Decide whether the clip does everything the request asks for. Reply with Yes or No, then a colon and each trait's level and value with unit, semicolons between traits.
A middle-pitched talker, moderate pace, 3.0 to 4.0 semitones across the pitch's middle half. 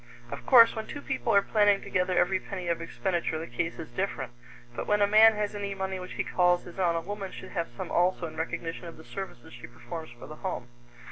No: medium, 180 Hz; fast, 240 wpm; average, 3.3 semitones